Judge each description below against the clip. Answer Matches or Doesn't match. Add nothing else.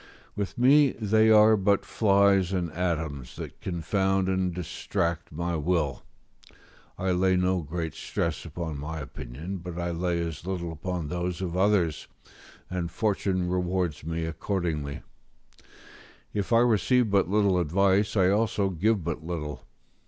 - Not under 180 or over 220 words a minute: Doesn't match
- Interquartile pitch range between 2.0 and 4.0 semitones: Matches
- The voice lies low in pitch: Matches